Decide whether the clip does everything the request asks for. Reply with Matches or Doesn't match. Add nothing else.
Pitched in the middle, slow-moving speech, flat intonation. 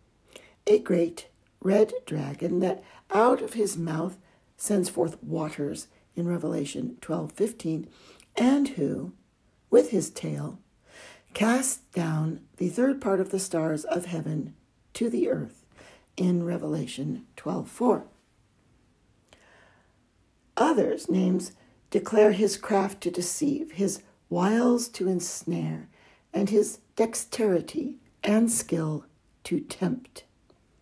Doesn't match